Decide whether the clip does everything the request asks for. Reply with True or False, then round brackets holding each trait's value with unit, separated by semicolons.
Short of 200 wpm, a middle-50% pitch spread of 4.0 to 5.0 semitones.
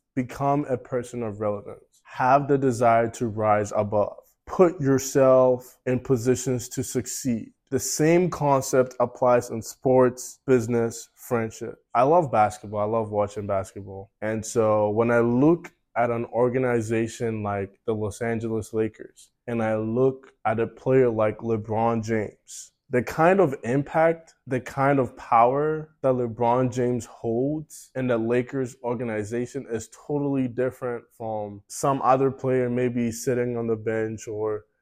False (145 wpm; 2.8 semitones)